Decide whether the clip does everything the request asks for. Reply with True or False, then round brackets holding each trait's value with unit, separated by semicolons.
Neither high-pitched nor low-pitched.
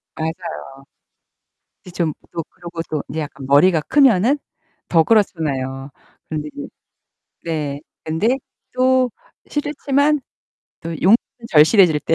True (165 Hz)